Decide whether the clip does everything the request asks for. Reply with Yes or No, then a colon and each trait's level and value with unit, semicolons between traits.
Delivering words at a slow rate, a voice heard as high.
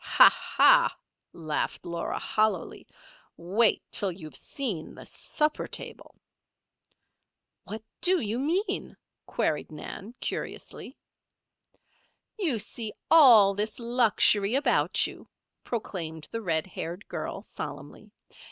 Yes: slow, 105 wpm; high, 215 Hz